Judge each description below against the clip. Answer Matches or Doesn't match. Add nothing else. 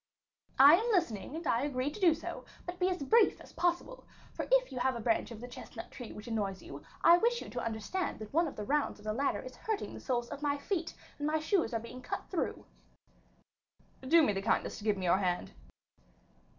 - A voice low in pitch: Doesn't match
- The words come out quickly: Matches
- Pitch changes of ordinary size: Doesn't match